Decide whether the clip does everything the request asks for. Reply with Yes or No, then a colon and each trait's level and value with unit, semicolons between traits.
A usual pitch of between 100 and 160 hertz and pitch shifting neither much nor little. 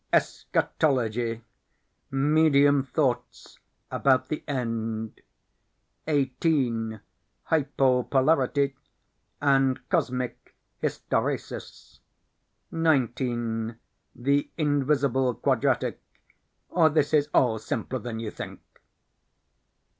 Yes: low, 135 Hz; average, 3.3 semitones